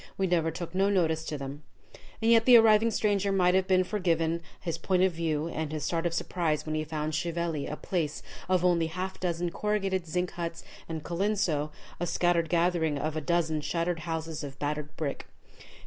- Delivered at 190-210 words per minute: Yes, average, 195 wpm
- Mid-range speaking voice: Yes, medium, 170 Hz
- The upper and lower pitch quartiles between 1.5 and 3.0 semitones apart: Yes, average, 2.7 semitones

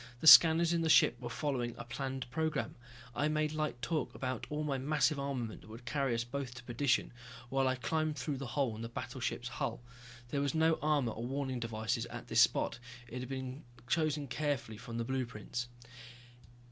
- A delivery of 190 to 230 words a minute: Yes, average, 195 wpm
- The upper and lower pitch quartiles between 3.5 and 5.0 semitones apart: Yes, average, 3.8 semitones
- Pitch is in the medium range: No, low, 130 Hz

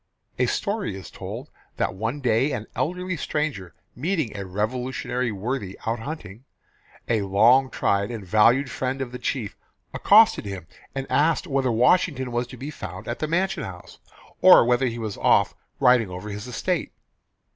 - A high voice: No, low, 125 Hz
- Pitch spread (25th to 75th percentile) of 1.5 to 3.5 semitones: No, average, 4.7 semitones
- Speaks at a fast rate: No, average, 165 wpm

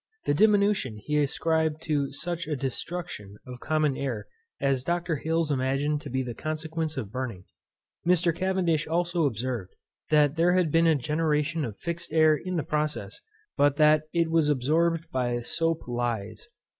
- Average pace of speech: Yes, average, 160 wpm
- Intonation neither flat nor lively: Yes, average, 4.0 semitones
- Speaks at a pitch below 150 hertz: No, medium, 155 Hz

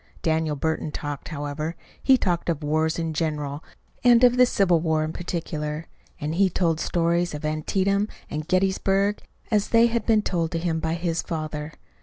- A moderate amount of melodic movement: Yes, average, 3.6 semitones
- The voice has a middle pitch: Yes, medium, 165 Hz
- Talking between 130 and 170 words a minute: No, average, 180 wpm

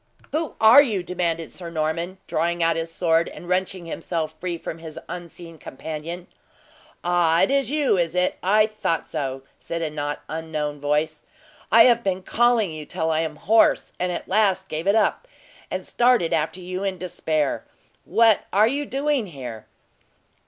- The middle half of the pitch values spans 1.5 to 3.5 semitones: No, average, 4.0 semitones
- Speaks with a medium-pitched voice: Yes, medium, 175 Hz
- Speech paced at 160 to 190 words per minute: Yes, average, 170 wpm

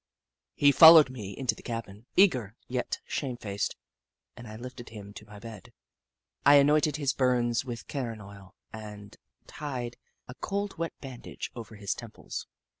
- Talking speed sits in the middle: Yes, average, 150 wpm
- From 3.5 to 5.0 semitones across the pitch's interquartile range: Yes, average, 4.6 semitones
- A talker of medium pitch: No, low, 120 Hz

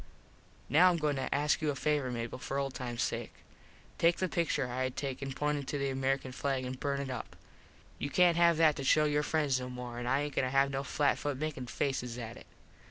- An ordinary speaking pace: No, fast, 235 wpm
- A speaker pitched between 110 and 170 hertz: Yes, medium, 140 Hz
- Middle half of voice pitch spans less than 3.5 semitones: Yes, narrow, 2.5 semitones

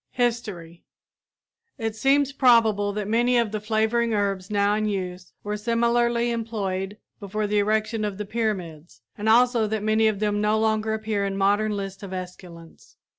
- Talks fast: No, average, 165 wpm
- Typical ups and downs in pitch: No, narrow, 2.1 semitones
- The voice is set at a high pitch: Yes, high, 215 Hz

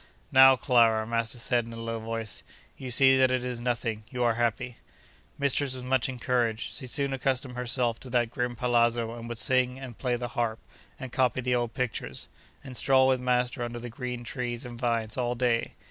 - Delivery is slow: No, average, 200 wpm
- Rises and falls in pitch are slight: Yes, narrow, 1.5 semitones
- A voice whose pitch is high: No, low, 125 Hz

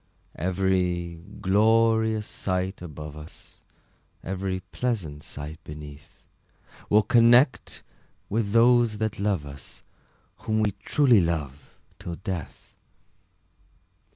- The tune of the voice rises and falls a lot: No, average, 5.0 semitones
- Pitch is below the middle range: Yes, very low, 95 Hz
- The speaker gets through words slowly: Yes, slow, 95 wpm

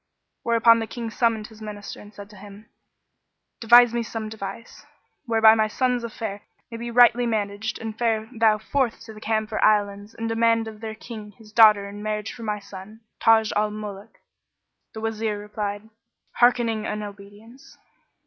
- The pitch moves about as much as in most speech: No, narrow, 1.5 semitones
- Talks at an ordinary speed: Yes, average, 170 wpm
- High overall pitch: Yes, high, 220 Hz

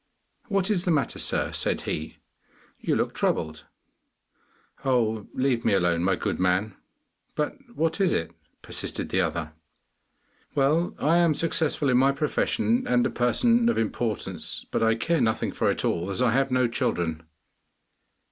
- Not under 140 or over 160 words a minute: Yes, average, 155 wpm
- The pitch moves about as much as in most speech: No, wide, 8.0 semitones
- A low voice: Yes, low, 125 Hz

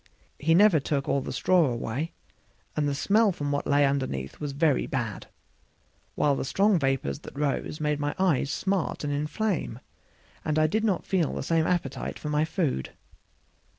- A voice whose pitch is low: No, medium, 150 Hz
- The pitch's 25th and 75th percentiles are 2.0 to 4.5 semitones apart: Yes, average, 3.6 semitones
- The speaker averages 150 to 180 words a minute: Yes, average, 175 wpm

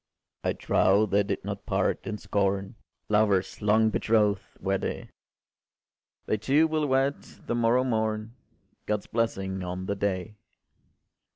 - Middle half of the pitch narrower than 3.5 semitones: Yes, average, 2.7 semitones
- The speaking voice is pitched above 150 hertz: No, low, 105 Hz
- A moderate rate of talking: No, slow, 130 wpm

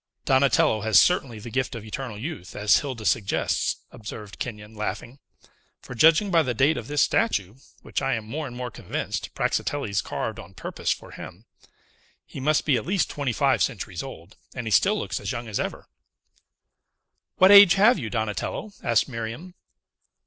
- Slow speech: No, average, 175 wpm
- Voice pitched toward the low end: Yes, low, 125 Hz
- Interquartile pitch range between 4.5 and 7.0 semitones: Yes, average, 5.3 semitones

